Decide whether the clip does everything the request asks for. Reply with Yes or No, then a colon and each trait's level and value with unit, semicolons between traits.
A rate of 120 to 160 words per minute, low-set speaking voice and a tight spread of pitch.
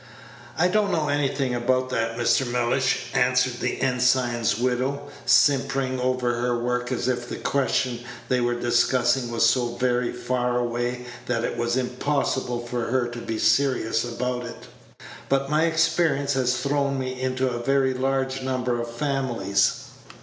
Yes: average, 155 wpm; low, 125 Hz; narrow, 1.8 semitones